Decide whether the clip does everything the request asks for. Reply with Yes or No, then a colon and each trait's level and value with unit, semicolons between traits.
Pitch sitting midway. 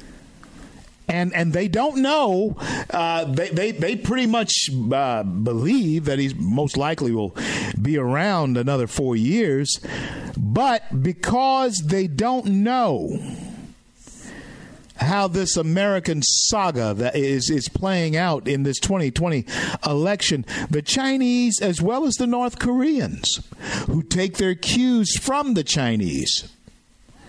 Yes: medium, 170 Hz